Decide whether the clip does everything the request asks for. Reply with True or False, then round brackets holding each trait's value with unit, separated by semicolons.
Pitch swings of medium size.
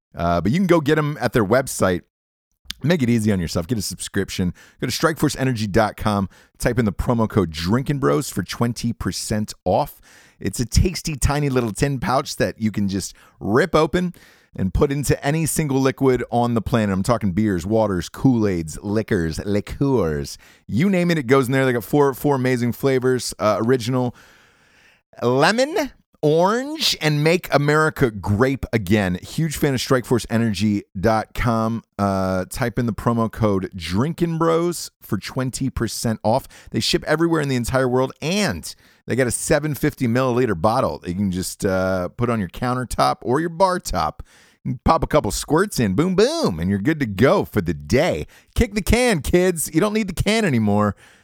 False (6.0 semitones)